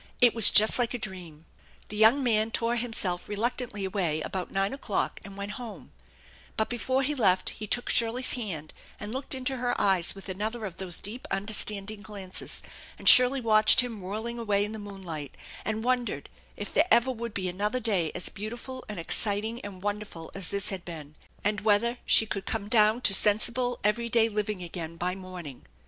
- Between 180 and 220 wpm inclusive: Yes, average, 190 wpm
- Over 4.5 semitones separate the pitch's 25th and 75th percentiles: No, average, 3.6 semitones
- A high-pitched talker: Yes, high, 210 Hz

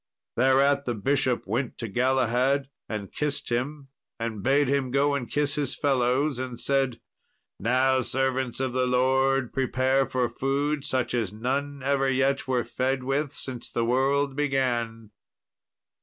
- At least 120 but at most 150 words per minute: Yes, average, 145 wpm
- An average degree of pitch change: No, narrow, 2.0 semitones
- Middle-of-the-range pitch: No, low, 130 Hz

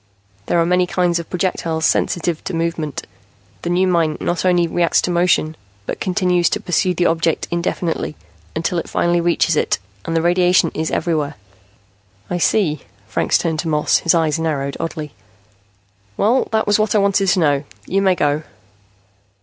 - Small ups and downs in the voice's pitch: Yes, narrow, 2.0 semitones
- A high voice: No, medium, 170 Hz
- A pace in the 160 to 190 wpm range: Yes, average, 170 wpm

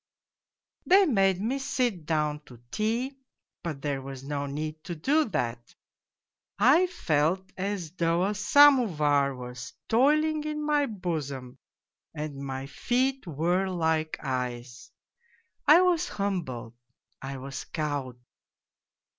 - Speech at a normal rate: No, slow, 120 wpm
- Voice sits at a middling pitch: Yes, medium, 170 Hz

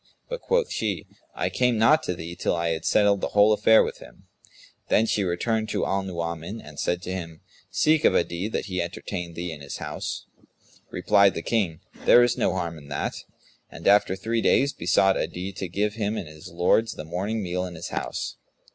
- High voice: No, very low, 95 Hz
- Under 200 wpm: No, fast, 205 wpm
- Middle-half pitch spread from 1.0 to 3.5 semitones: No, average, 4.2 semitones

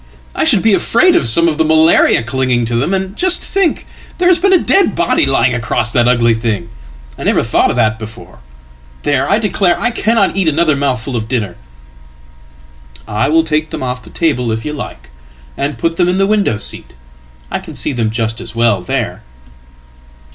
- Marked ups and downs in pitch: Yes, wide, 7.8 semitones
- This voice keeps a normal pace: Yes, average, 185 wpm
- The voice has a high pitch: No, low, 125 Hz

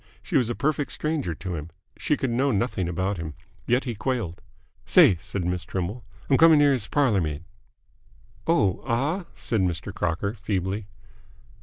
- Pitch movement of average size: No, wide, 6.8 semitones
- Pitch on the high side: No, low, 105 Hz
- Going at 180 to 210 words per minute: No, average, 165 wpm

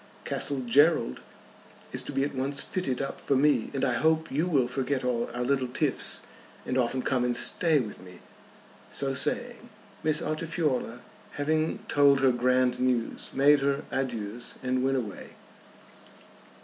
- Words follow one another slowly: No, average, 155 wpm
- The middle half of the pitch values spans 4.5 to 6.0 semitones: No, average, 2.7 semitones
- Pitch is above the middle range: No, low, 135 Hz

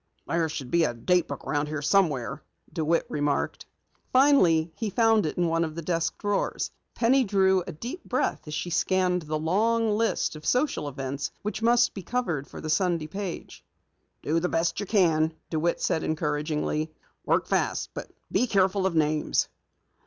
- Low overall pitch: No, medium, 170 Hz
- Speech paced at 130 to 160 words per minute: No, average, 175 wpm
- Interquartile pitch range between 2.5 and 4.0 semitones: No, average, 4.8 semitones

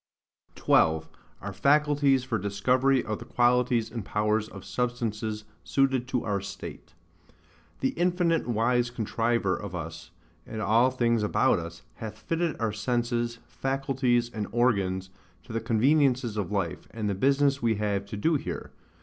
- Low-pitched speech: Yes, low, 115 Hz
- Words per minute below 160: Yes, average, 150 wpm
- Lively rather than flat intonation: No, average, 3.7 semitones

